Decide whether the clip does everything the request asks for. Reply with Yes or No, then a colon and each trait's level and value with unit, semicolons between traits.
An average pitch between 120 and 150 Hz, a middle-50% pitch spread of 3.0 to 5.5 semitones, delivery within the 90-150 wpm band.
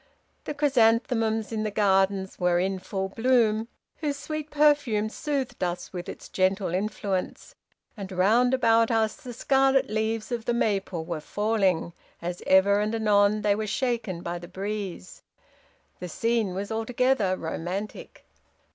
No: high, 215 Hz; average, 3.6 semitones; average, 145 wpm